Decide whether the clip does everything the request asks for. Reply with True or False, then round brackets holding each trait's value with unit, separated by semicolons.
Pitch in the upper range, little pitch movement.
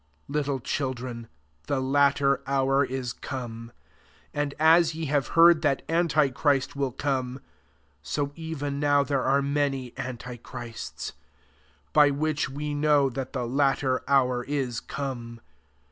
False (140 Hz; 2.2 semitones)